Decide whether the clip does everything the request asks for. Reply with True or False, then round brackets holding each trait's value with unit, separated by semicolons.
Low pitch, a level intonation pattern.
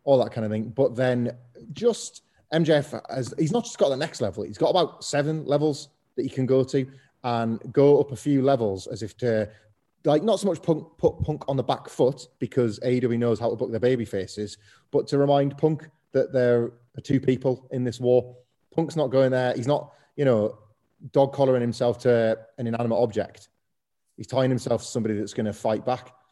False (125 Hz; 3.4 semitones)